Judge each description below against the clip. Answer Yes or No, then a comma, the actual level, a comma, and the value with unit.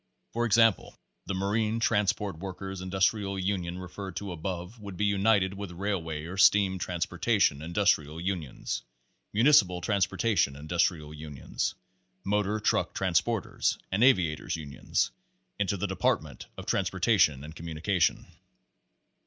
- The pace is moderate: No, slow, 130 wpm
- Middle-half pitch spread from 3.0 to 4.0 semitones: Yes, average, 3.3 semitones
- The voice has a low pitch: Yes, very low, 95 Hz